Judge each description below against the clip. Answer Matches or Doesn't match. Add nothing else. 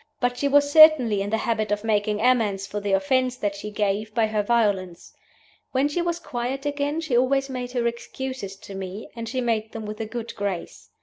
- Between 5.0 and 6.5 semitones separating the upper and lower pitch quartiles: Doesn't match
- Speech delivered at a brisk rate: Matches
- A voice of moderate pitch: Doesn't match